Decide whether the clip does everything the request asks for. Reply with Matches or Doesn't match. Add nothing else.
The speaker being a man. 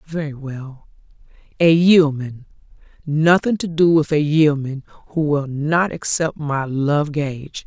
Doesn't match